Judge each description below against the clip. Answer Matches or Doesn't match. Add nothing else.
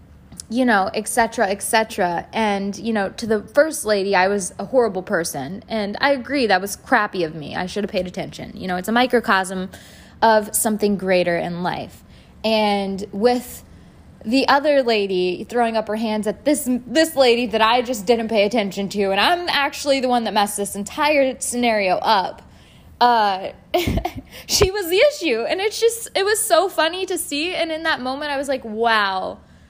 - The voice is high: Matches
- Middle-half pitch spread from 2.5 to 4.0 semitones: Doesn't match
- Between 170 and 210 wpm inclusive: Matches